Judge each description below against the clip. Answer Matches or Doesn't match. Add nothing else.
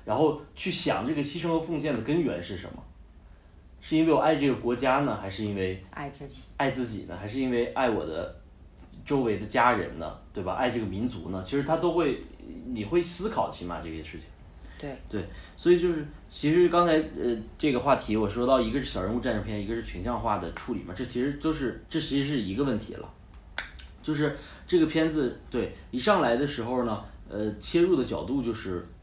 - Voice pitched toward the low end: Matches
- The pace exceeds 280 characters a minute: Matches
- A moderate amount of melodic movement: Doesn't match